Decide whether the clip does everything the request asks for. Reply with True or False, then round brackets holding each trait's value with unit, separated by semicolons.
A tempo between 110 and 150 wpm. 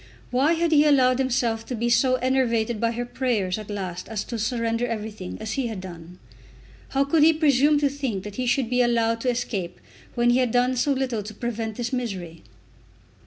False (205 wpm)